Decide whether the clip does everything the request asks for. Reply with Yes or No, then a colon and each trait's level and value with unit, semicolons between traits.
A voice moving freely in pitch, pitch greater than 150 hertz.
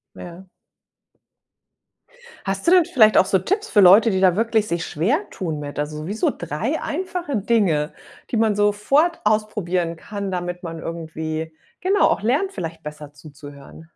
Yes: wide, 5.8 semitones; high, 190 Hz